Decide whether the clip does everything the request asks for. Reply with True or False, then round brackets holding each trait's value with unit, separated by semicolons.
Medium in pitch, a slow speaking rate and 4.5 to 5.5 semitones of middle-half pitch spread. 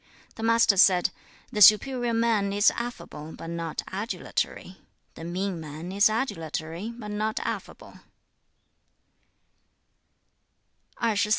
False (200 Hz; 100 wpm; 4.9 semitones)